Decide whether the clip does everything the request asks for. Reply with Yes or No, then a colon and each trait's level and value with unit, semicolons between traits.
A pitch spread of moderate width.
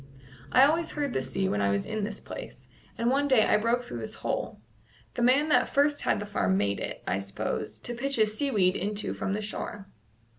No: wide, 6.5 semitones